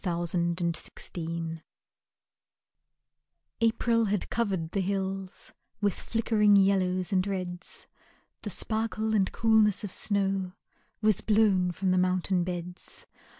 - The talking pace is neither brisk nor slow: No, slow, 110 wpm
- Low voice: No, high, 190 Hz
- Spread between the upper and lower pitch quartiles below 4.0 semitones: Yes, average, 2.8 semitones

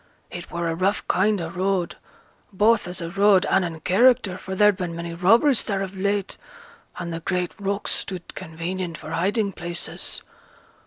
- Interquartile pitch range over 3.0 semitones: No, average, 2.7 semitones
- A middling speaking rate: Yes, average, 170 wpm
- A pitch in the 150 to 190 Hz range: Yes, medium, 185 Hz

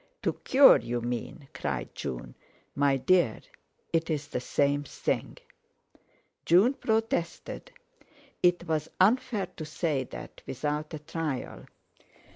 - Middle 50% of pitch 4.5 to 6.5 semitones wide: Yes, average, 4.9 semitones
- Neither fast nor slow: No, slow, 110 wpm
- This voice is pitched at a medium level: Yes, medium, 155 Hz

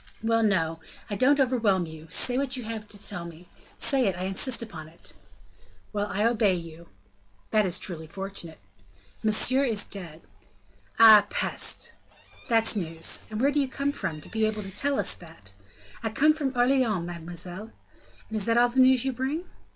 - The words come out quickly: No, average, 180 wpm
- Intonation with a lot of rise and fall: Yes, wide, 6.1 semitones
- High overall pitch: Yes, high, 215 Hz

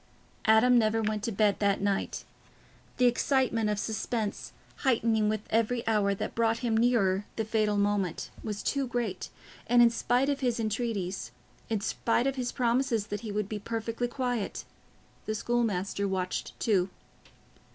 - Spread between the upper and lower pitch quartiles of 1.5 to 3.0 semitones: Yes, average, 2.7 semitones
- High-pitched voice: Yes, high, 220 Hz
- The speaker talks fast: No, average, 155 wpm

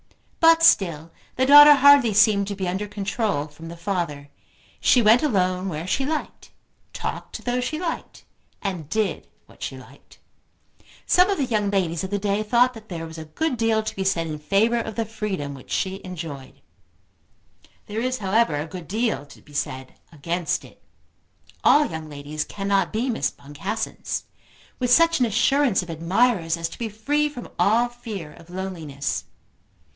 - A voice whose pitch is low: No, high, 200 Hz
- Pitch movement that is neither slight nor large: No, wide, 6.4 semitones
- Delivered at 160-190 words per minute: Yes, average, 175 wpm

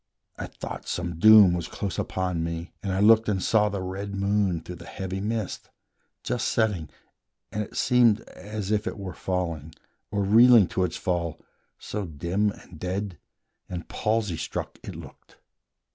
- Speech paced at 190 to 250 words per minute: No, average, 165 wpm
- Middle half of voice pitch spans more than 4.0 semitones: No, average, 3.1 semitones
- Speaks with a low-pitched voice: Yes, very low, 95 Hz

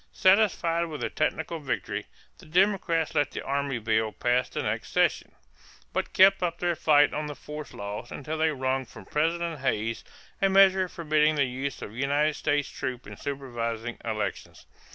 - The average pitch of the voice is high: No, medium, 145 Hz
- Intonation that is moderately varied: Yes, average, 4.7 semitones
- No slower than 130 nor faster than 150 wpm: No, average, 170 wpm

